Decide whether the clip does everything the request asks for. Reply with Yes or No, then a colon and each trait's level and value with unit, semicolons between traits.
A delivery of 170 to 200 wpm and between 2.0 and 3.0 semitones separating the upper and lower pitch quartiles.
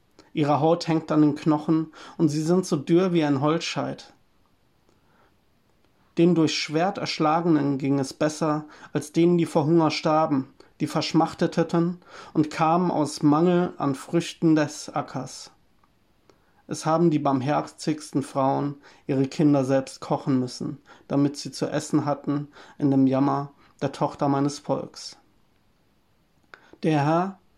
No: average, 135 wpm; narrow, 2.4 semitones